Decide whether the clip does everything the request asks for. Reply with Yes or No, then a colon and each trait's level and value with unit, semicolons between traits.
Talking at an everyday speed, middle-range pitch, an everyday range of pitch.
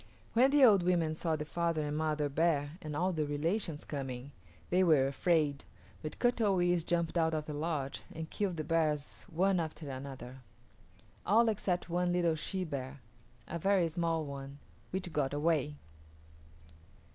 Yes: average, 165 wpm; medium, 160 Hz; average, 3.2 semitones